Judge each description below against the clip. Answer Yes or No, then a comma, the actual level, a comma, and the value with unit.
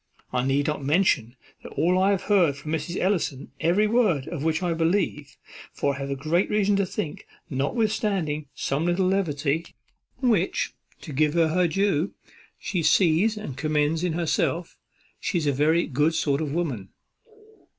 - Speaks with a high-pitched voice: No, medium, 160 Hz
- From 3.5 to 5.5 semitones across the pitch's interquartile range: Yes, average, 4.2 semitones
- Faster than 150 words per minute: Yes, average, 165 wpm